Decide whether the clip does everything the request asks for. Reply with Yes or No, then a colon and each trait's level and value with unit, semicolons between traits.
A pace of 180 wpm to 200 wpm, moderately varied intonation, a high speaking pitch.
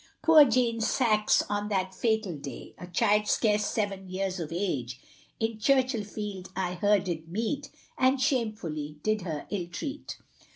No: average, 150 wpm; average, 4.1 semitones; high, 205 Hz